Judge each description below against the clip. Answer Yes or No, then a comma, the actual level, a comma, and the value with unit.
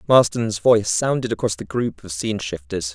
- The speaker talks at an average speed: Yes, average, 185 wpm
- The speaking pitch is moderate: No, low, 100 Hz